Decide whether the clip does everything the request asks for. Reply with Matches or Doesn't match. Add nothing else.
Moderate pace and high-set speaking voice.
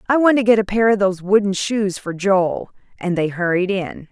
Doesn't match